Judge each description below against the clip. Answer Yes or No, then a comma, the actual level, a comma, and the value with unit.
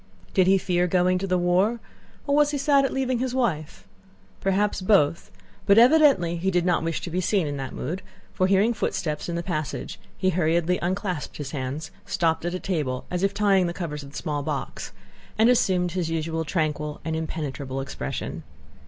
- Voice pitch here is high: No, medium, 180 Hz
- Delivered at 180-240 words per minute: Yes, average, 190 wpm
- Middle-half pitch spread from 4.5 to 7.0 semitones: No, average, 3.7 semitones